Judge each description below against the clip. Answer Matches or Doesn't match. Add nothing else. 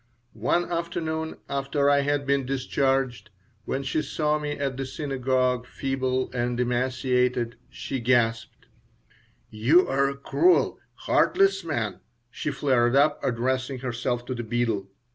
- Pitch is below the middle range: Matches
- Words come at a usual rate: Doesn't match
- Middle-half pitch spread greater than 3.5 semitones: Doesn't match